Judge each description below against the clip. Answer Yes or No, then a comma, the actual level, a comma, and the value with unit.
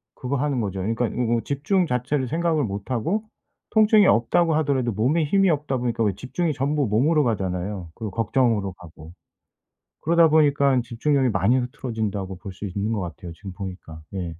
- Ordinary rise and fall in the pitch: No, wide, 6.6 semitones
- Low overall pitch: Yes, low, 120 Hz